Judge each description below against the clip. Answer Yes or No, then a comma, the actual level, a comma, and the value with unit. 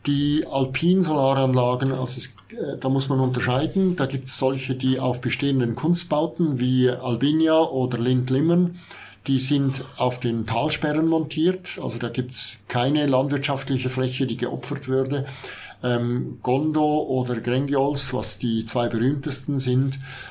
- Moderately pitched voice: No, low, 130 Hz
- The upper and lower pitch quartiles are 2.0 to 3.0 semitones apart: Yes, narrow, 2.5 semitones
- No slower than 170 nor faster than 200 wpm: No, average, 135 wpm